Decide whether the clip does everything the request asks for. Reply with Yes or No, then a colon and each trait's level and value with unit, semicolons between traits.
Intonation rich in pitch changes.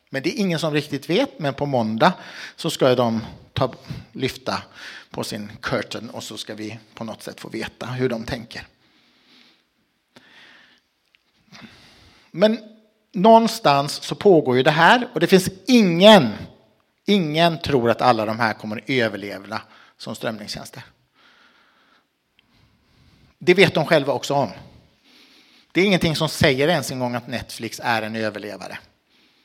Yes: wide, 7.8 semitones